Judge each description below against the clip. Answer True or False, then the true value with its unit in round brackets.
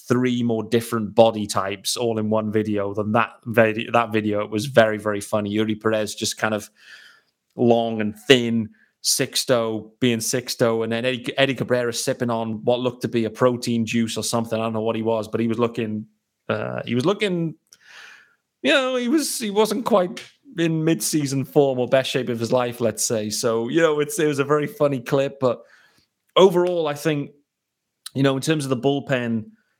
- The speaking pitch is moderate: False (120 Hz)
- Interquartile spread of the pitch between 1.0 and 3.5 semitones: False (4.1 semitones)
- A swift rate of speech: False (195 wpm)